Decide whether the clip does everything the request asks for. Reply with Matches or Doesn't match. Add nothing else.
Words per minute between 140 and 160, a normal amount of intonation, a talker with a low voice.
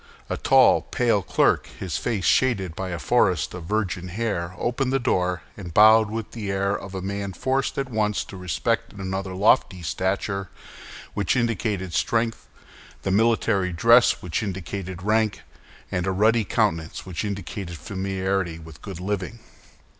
Matches